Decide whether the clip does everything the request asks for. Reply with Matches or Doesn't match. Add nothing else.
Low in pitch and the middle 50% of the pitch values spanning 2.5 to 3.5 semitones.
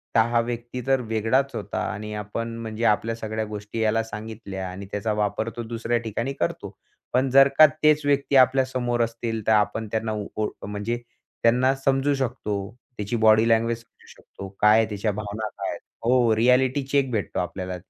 Matches